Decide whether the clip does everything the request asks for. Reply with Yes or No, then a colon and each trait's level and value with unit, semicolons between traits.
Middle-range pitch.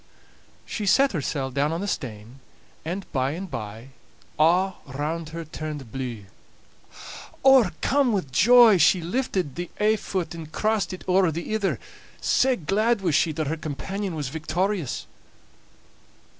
Yes: medium, 170 Hz